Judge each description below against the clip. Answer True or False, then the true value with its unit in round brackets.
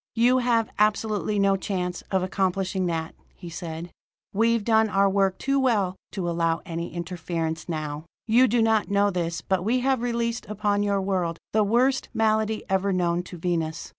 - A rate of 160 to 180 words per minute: True (170 wpm)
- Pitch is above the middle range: True (195 Hz)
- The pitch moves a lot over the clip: False (4.2 semitones)